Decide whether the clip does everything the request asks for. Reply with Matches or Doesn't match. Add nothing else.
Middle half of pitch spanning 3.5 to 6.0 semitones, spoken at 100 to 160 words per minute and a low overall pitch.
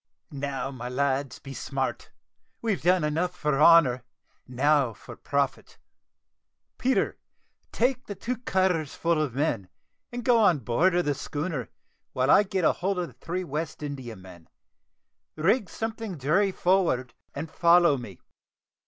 Doesn't match